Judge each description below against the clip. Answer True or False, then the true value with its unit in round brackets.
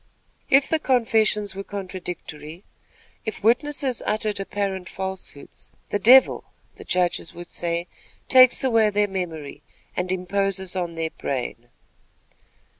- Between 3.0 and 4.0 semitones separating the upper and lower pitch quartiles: True (3.6 semitones)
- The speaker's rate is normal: False (115 wpm)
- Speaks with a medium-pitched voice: False (195 Hz)